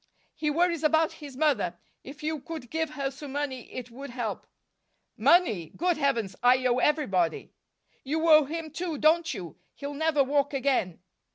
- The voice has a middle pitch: No, very high, 285 Hz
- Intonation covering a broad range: No, average, 3.8 semitones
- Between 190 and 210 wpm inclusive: No, average, 165 wpm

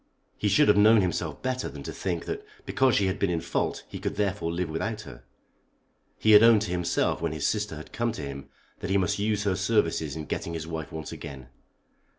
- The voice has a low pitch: Yes, very low, 95 Hz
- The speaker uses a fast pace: Yes, fast, 225 wpm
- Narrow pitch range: No, average, 4.7 semitones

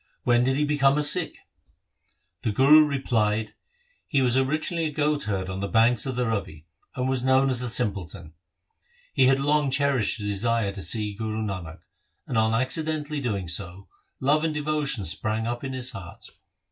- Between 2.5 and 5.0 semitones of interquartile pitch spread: No, wide, 5.4 semitones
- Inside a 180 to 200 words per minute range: Yes, average, 185 wpm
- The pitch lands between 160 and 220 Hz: No, low, 125 Hz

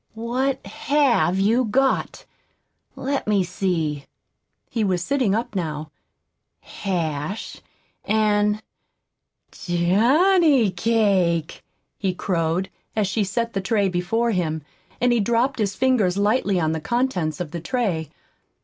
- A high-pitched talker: Yes, high, 200 Hz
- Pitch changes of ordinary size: Yes, average, 4.9 semitones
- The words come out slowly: Yes, slow, 120 wpm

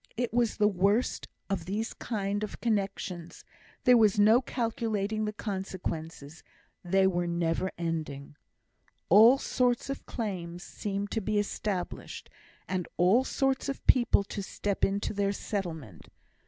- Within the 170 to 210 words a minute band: No, average, 140 wpm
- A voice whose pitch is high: Yes, high, 200 Hz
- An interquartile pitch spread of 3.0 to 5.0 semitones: Yes, average, 3.8 semitones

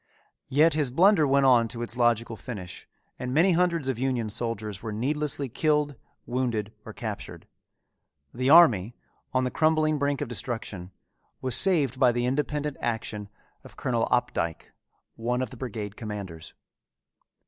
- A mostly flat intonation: No, average, 4.4 semitones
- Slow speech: No, average, 150 wpm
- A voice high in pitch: No, low, 125 Hz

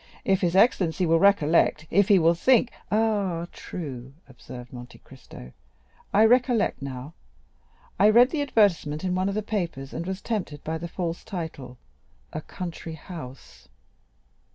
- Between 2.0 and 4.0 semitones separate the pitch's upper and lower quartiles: No, average, 5.2 semitones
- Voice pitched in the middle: Yes, medium, 170 Hz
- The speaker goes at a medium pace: Yes, average, 145 wpm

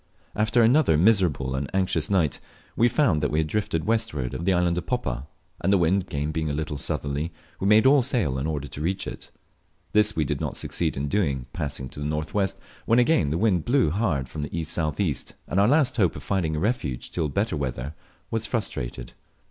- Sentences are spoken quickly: Yes, fast, 210 wpm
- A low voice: Yes, very low, 85 Hz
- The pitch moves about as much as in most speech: No, wide, 6.5 semitones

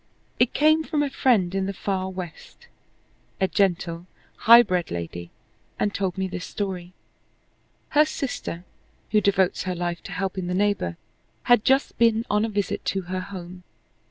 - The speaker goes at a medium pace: Yes, average, 160 wpm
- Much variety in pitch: No, average, 3.4 semitones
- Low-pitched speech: No, high, 190 Hz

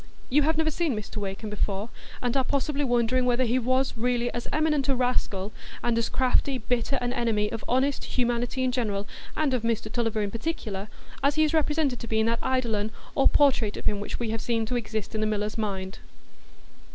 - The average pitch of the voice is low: No, high, 240 Hz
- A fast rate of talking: Yes, fast, 210 wpm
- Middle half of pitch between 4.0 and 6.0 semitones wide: No, average, 3.3 semitones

